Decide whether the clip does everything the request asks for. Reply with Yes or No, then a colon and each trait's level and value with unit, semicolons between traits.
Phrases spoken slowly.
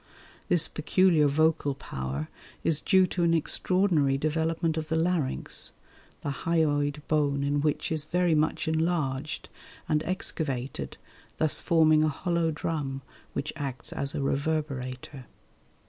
Yes: slow, 130 wpm